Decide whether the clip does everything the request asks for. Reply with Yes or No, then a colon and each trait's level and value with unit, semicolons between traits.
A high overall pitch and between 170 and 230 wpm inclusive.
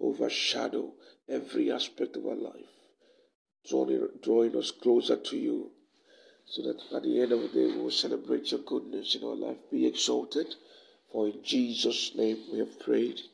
No: very high, 325 Hz; average, 160 wpm